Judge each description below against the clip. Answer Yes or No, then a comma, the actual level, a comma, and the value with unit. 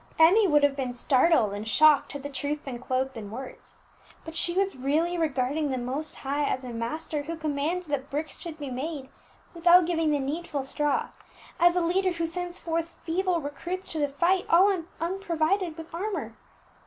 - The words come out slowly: No, average, 185 wpm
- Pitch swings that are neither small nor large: Yes, average, 3.8 semitones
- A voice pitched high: Yes, very high, 310 Hz